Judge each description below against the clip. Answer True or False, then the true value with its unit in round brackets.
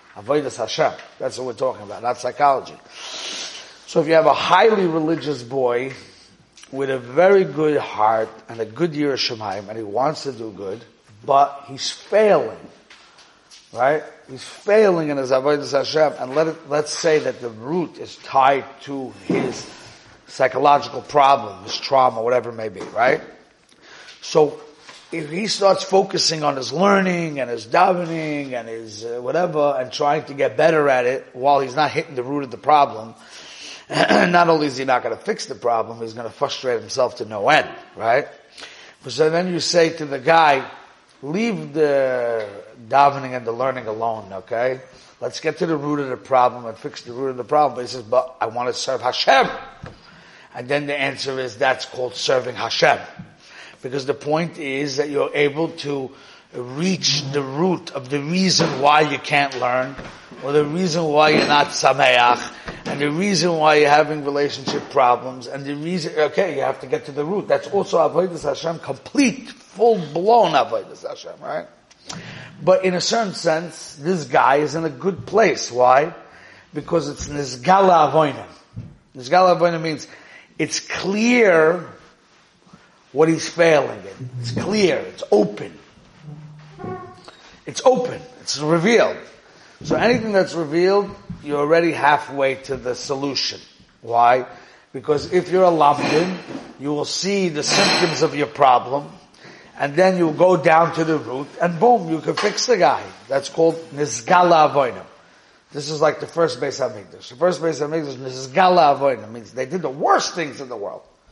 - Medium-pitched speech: True (150 Hz)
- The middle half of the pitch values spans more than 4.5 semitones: False (4.2 semitones)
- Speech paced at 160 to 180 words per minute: True (170 wpm)